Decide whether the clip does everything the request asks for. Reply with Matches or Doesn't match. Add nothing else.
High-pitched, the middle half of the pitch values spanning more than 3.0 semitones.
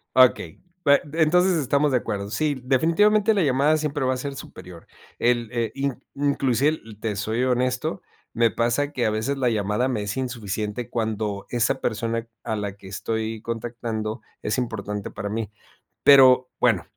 Doesn't match